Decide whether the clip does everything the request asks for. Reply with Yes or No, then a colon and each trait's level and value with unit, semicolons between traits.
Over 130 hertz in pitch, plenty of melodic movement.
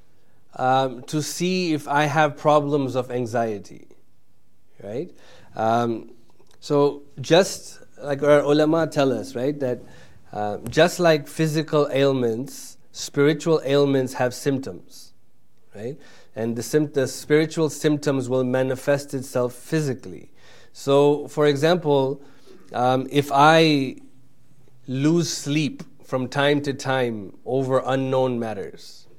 No: medium, 140 Hz; average, 2.7 semitones